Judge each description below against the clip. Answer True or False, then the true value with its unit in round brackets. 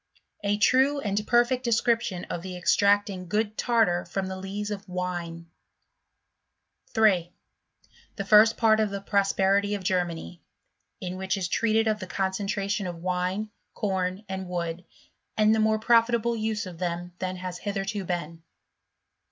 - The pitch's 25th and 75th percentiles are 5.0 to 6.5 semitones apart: False (2.9 semitones)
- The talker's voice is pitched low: False (195 Hz)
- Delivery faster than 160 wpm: False (150 wpm)